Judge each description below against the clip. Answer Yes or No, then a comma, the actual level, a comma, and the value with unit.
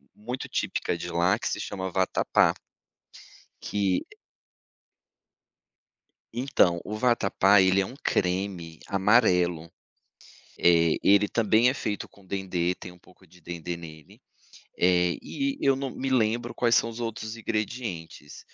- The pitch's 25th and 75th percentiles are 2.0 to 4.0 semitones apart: No, average, 4.7 semitones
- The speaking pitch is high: No, very low, 95 Hz